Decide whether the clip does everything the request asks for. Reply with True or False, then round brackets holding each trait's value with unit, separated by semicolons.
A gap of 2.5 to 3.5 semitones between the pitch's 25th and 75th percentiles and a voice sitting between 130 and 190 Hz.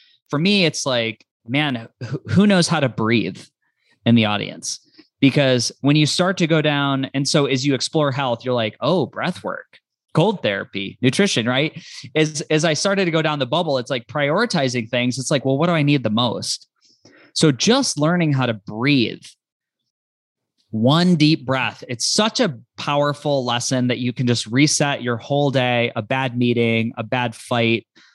False (4.2 semitones; 135 Hz)